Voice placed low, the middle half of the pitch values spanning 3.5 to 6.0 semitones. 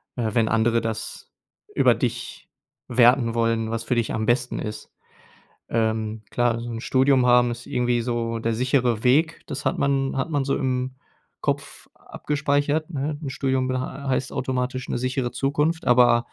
No: low, 125 Hz; narrow, 2.6 semitones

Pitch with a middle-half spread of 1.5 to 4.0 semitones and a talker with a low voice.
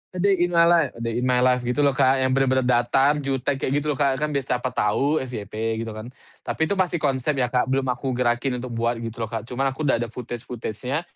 Yes: narrow, 2.6 semitones; low, 130 Hz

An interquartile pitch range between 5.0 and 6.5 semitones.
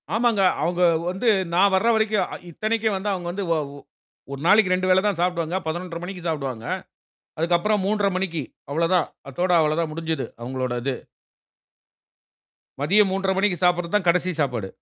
No: average, 3.5 semitones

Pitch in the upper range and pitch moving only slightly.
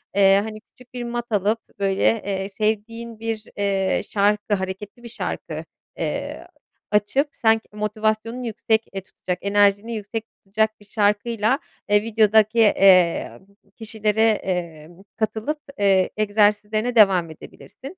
Yes: high, 210 Hz; narrow, 2.0 semitones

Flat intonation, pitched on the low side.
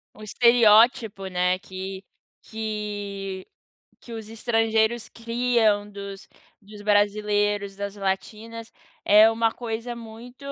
No: narrow, 2.1 semitones; high, 215 Hz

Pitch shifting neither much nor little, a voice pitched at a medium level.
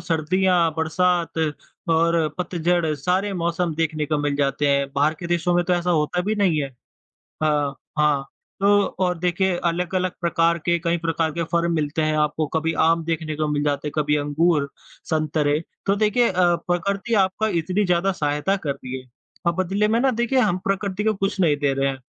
Yes: average, 3.4 semitones; medium, 170 Hz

